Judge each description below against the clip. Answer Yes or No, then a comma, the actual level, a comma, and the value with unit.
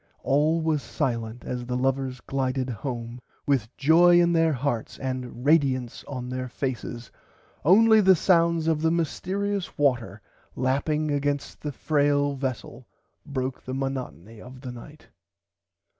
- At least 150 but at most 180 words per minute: No, slow, 135 wpm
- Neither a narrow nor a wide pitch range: Yes, average, 3.8 semitones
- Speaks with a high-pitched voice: No, low, 135 Hz